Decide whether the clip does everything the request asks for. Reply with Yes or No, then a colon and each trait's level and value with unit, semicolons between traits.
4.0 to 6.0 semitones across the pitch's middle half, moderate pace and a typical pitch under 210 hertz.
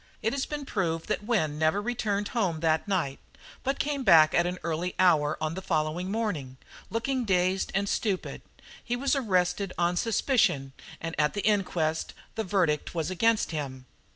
Yes: average, 5.3 semitones; average, 170 wpm; medium, 185 Hz